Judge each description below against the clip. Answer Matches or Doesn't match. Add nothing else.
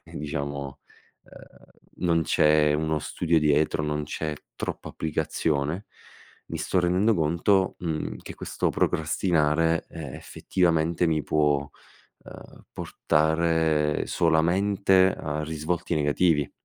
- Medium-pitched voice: Doesn't match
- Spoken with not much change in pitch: Matches